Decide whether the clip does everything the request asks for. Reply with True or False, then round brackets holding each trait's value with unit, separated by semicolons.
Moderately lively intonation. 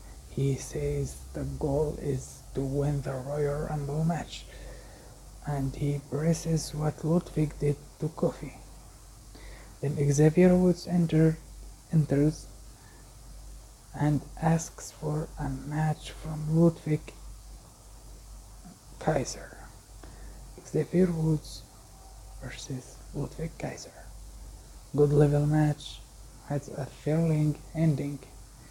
True (3.7 semitones)